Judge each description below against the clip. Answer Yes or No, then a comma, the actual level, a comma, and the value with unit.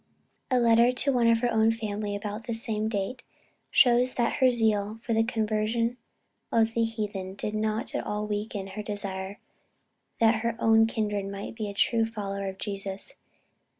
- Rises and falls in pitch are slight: Yes, narrow, 2.0 semitones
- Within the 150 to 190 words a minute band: Yes, average, 175 wpm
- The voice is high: Yes, high, 220 Hz